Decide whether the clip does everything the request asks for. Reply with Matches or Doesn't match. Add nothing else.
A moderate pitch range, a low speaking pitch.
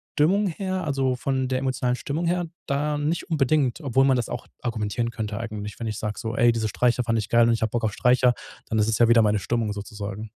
Matches